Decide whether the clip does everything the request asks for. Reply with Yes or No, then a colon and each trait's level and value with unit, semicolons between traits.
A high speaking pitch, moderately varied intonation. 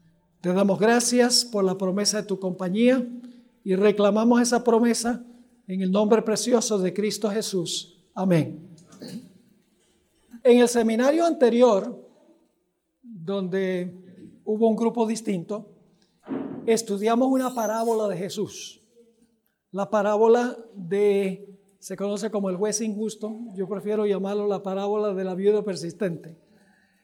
Yes: high, 210 Hz; average, 3.1 semitones